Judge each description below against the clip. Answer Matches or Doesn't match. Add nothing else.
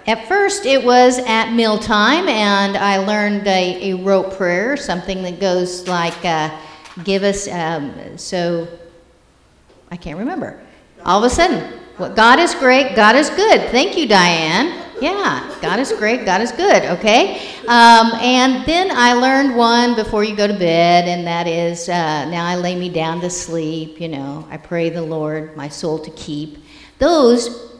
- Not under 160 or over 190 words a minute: Matches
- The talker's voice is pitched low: Doesn't match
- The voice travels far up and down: Matches